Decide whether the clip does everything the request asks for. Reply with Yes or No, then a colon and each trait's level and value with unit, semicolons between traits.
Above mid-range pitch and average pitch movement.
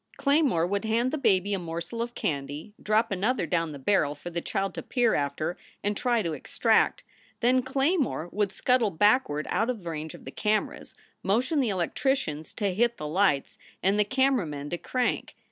No: high, 205 Hz; wide, 6.5 semitones